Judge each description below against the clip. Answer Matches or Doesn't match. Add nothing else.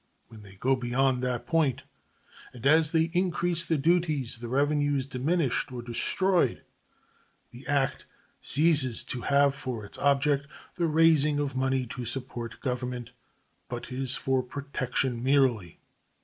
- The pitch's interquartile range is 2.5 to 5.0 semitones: Matches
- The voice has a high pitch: Doesn't match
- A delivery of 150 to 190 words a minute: Doesn't match